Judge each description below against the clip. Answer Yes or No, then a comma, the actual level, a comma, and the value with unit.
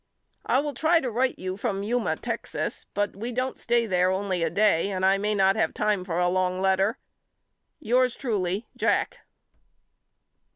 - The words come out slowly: No, average, 170 wpm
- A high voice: Yes, high, 205 Hz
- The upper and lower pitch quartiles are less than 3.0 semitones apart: No, average, 4.2 semitones